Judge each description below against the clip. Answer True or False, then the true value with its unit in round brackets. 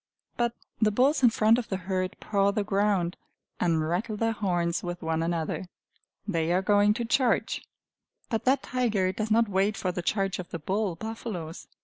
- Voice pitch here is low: False (200 Hz)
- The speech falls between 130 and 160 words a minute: False (185 wpm)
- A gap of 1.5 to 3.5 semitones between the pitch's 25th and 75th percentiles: False (4.0 semitones)